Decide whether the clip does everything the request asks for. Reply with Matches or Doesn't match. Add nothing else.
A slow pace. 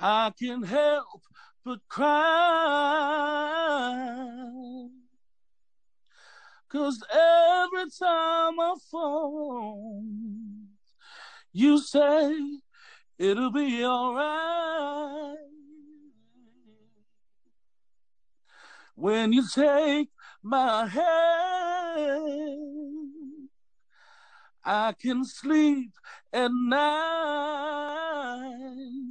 Matches